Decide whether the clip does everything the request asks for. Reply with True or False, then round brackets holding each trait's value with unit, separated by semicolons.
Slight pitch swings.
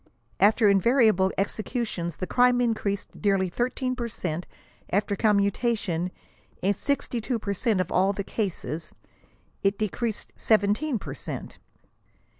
False (3.6 semitones)